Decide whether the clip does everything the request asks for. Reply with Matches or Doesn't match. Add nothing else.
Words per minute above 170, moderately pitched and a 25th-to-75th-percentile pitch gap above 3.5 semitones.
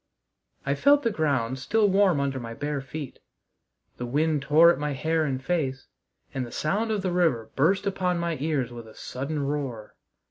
Matches